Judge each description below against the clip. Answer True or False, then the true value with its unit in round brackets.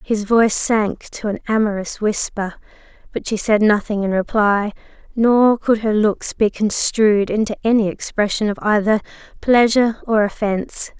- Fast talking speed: False (145 wpm)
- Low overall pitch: False (215 Hz)